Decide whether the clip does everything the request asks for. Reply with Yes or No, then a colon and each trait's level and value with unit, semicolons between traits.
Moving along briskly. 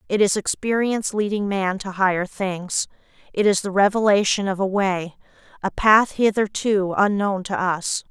No: average, 155 wpm